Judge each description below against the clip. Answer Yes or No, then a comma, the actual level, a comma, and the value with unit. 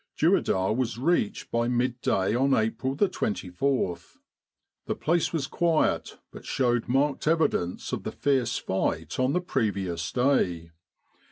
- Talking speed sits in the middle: No, slow, 125 wpm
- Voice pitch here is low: Yes, low, 125 Hz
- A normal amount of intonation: No, wide, 6.0 semitones